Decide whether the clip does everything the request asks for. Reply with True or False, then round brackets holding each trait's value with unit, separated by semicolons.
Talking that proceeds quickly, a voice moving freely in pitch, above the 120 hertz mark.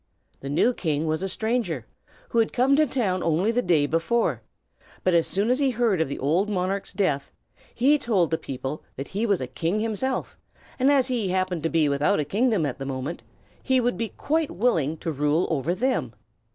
True (210 wpm; 7.2 semitones; 185 Hz)